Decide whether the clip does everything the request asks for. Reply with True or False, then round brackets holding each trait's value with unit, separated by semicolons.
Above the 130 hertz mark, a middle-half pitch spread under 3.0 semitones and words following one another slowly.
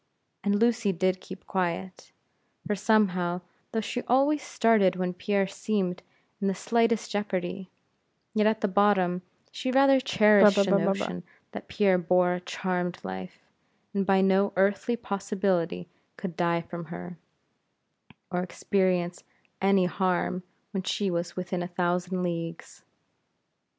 True (190 Hz; 2.4 semitones; 130 wpm)